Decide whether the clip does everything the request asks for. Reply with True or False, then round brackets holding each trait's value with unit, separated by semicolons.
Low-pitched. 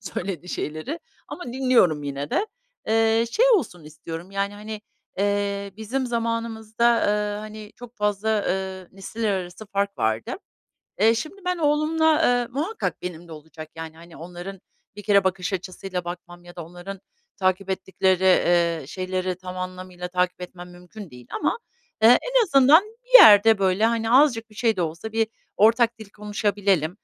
False (200 Hz)